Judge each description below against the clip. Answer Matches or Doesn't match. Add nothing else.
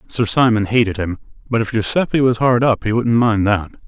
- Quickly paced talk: Matches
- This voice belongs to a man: Matches